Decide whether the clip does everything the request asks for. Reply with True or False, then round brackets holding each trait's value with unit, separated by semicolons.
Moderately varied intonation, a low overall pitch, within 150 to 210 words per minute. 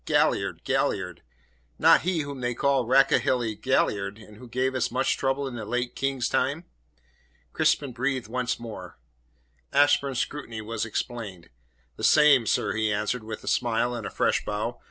True (3.3 semitones; 125 Hz; 160 wpm)